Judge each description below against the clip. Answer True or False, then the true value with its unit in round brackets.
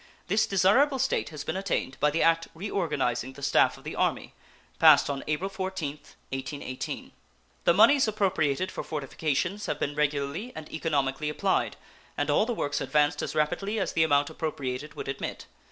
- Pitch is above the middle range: False (155 Hz)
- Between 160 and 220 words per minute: True (170 wpm)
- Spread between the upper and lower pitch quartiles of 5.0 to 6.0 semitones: True (5.3 semitones)